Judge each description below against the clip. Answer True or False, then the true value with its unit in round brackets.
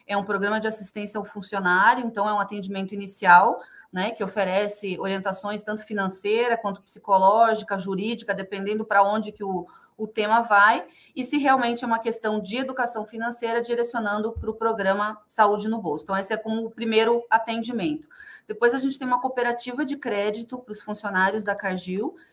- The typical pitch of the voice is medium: False (215 Hz)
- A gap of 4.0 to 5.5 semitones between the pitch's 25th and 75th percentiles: False (2.6 semitones)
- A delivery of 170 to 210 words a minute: True (175 wpm)